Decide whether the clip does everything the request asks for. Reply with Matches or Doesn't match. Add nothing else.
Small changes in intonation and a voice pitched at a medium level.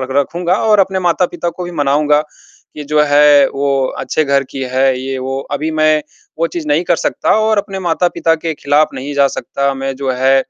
Doesn't match